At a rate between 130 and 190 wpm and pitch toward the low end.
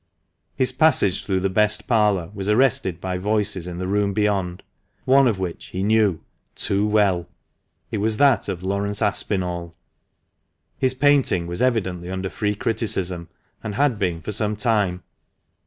Yes: average, 155 wpm; low, 100 Hz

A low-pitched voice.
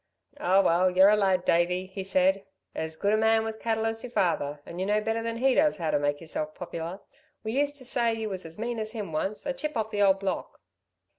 No: high, 200 Hz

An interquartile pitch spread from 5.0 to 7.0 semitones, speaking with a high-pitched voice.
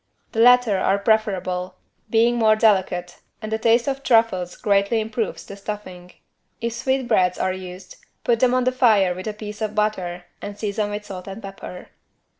No: average, 3.4 semitones; high, 210 Hz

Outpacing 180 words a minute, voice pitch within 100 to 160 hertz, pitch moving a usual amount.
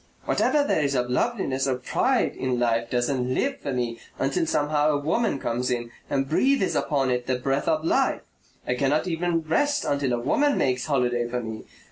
Yes: average, 190 wpm; low, 135 Hz; average, 4.1 semitones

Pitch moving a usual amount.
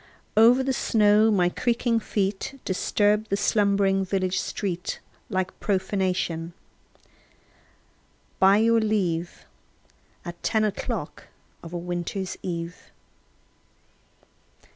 Yes: average, 3.0 semitones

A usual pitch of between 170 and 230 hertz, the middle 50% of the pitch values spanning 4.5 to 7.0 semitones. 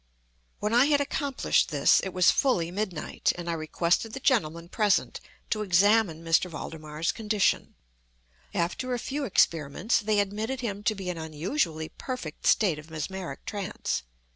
Yes: high, 190 Hz; average, 5.2 semitones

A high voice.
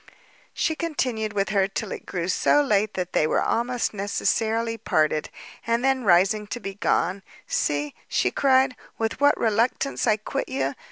Yes: high, 215 Hz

